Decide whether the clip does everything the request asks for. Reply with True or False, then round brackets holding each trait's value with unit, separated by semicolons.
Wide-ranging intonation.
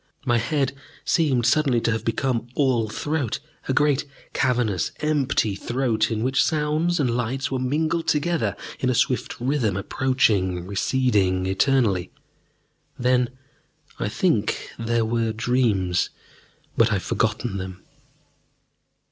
False (3.8 semitones)